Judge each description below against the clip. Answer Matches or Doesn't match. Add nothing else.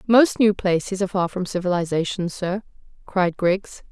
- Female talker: Matches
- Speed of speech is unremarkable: Matches